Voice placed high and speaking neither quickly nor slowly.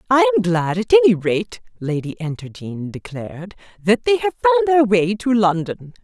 Yes: high, 195 Hz; average, 170 wpm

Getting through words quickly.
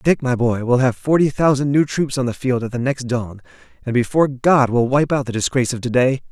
Yes: fast, 245 wpm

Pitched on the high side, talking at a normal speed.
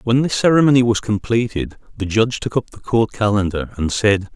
No: low, 110 Hz; average, 195 wpm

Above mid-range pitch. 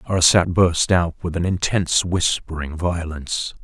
No: very low, 85 Hz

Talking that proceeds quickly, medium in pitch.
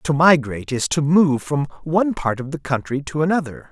Yes: fast, 210 wpm; medium, 150 Hz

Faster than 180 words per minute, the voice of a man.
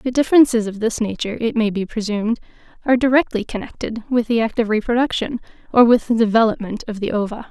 No: average, 190 wpm; female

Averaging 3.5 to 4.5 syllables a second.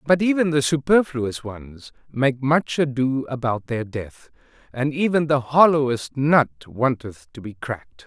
Yes: 4.2 syllables/s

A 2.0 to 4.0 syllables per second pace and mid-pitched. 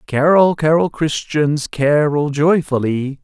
Yes: 3.6 syllables/s; medium, 150 Hz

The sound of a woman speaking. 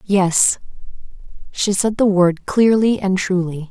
Yes: female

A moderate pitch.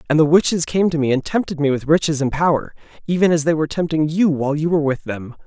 Yes: medium, 155 Hz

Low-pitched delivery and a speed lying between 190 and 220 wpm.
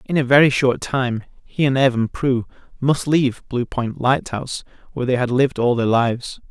Yes: low, 130 Hz; fast, 205 wpm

